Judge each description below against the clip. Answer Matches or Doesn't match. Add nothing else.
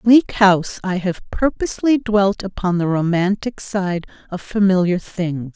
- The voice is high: Matches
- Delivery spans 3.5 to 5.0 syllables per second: Matches